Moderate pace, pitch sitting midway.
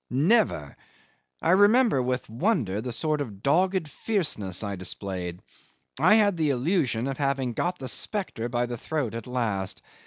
No: average, 155 wpm; low, 130 Hz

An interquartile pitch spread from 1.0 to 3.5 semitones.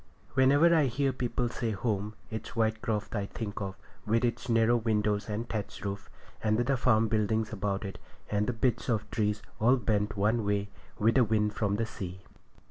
Yes: narrow, 2.4 semitones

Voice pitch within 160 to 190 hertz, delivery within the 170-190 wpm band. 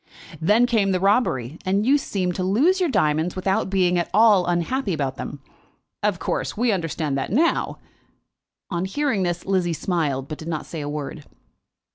Yes: medium, 185 Hz; average, 175 wpm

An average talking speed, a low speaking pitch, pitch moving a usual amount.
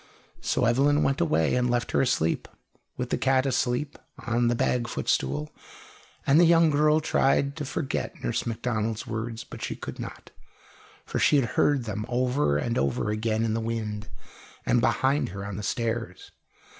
Yes: average, 170 wpm; low, 120 Hz; average, 3.7 semitones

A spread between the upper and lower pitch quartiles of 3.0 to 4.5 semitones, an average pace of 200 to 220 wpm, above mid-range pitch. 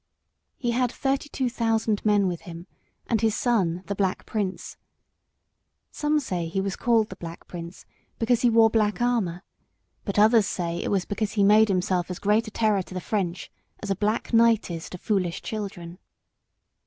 No: average, 3.7 semitones; average, 180 wpm; high, 210 Hz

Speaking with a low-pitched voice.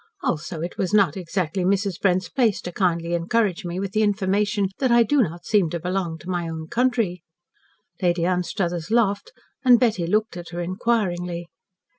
No: medium, 185 Hz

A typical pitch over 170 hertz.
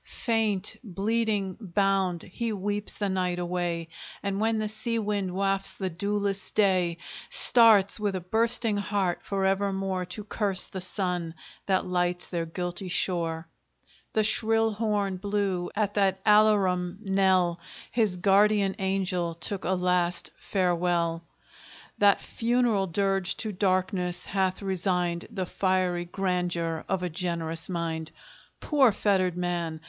Yes: high, 190 Hz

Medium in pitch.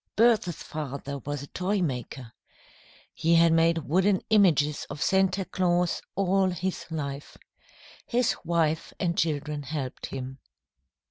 Yes: medium, 165 Hz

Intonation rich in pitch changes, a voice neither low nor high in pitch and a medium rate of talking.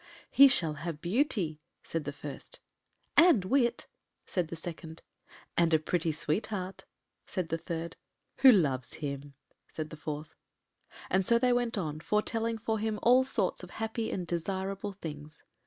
Yes: wide, 5.9 semitones; medium, 180 Hz; average, 155 wpm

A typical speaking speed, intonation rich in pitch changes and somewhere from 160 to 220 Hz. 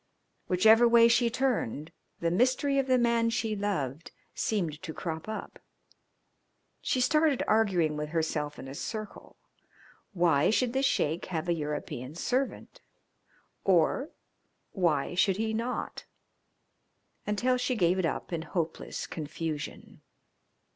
No: slow, 125 wpm; wide, 6.6 semitones; high, 190 Hz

